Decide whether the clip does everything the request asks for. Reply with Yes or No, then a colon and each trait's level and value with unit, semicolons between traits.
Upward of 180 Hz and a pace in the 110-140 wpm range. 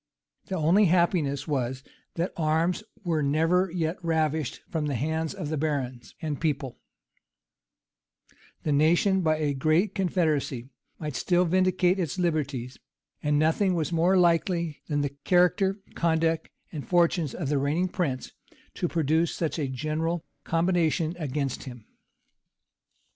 No: medium, 160 Hz; slow, 135 wpm